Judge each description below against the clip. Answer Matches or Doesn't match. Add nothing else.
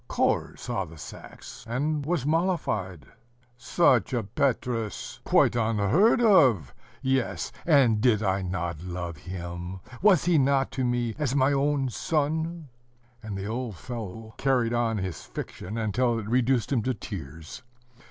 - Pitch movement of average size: Doesn't match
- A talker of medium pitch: Doesn't match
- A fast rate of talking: Doesn't match